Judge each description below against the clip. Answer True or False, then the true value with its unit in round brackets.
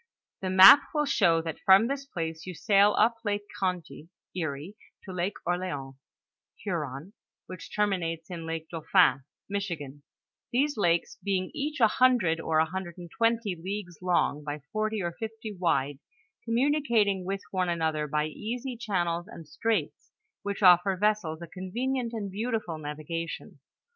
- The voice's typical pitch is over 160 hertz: True (185 Hz)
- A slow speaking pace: False (150 wpm)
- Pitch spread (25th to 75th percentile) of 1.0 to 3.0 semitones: False (4.6 semitones)